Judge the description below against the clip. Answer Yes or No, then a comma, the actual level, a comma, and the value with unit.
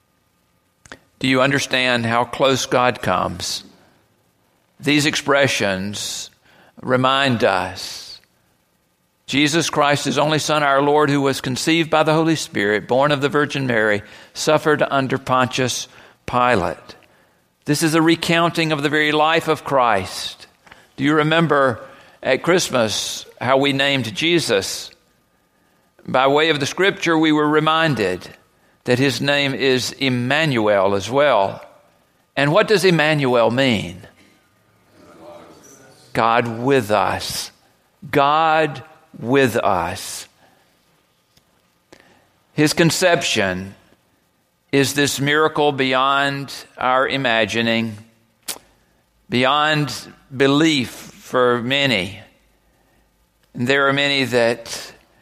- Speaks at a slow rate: Yes, slow, 105 wpm